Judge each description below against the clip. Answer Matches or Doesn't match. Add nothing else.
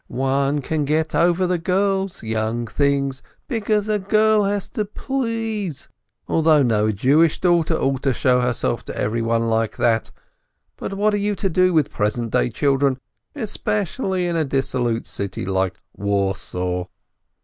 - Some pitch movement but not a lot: Doesn't match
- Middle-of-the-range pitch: Matches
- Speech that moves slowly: Doesn't match